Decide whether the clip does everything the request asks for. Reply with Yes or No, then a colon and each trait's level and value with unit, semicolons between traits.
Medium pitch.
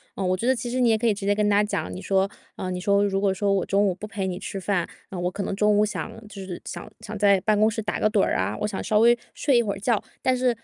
No: high, 205 Hz